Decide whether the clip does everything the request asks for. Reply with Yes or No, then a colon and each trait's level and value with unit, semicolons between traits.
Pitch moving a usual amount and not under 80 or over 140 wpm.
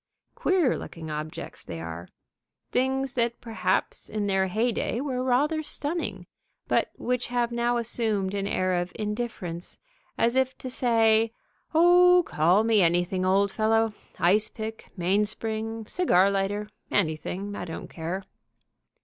Yes: average, 4.5 semitones; slow, 135 wpm